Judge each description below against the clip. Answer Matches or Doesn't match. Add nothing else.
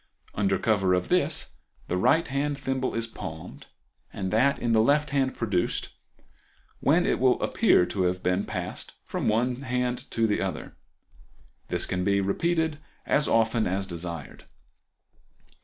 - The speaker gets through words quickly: Doesn't match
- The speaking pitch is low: Matches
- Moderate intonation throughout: Doesn't match